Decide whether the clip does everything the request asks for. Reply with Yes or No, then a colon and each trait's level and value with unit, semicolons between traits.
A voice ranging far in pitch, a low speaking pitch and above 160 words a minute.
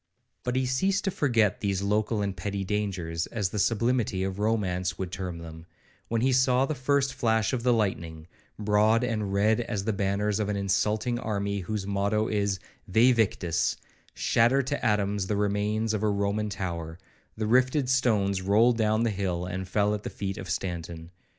No: average, 3.0 semitones; low, 105 Hz; average, 180 wpm